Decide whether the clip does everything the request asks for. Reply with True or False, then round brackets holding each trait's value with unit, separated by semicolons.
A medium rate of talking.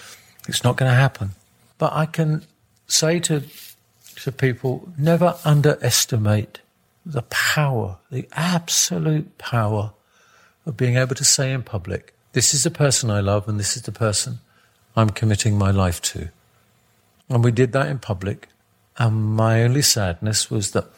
True (150 wpm)